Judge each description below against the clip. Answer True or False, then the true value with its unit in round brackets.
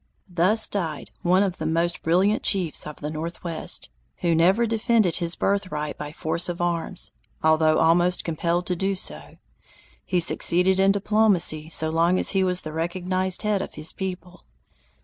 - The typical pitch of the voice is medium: True (175 Hz)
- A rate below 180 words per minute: True (165 wpm)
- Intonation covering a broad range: False (2.8 semitones)